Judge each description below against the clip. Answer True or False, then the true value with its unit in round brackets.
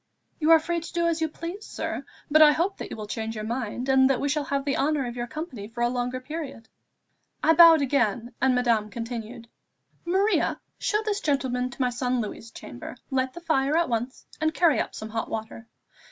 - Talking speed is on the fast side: True (215 wpm)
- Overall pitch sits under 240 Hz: False (265 Hz)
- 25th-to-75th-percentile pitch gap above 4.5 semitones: True (5.0 semitones)